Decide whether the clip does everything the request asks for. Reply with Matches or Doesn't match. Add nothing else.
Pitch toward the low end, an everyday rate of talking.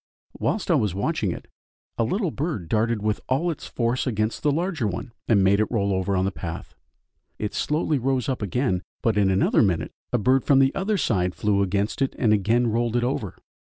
Doesn't match